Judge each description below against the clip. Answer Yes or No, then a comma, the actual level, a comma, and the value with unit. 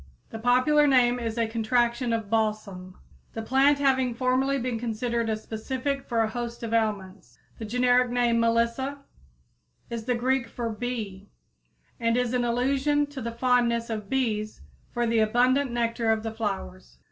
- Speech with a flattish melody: Yes, narrow, 2.1 semitones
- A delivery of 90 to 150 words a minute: No, average, 160 wpm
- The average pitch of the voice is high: Yes, high, 235 Hz